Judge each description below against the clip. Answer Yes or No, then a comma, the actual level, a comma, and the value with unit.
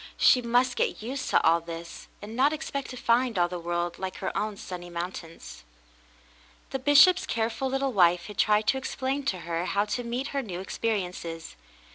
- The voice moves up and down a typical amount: No, wide, 6.7 semitones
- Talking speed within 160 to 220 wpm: Yes, average, 185 wpm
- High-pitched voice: Yes, high, 215 Hz